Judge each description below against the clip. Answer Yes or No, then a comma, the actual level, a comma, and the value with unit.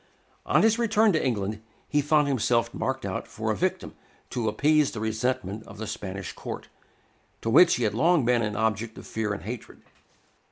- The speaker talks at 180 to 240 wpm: Yes, average, 190 wpm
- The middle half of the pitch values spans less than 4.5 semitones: No, average, 5.1 semitones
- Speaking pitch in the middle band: No, low, 115 Hz